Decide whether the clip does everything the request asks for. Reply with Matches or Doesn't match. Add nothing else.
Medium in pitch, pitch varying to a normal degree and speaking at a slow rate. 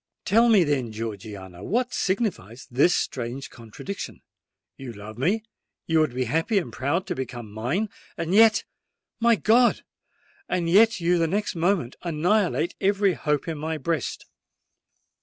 Doesn't match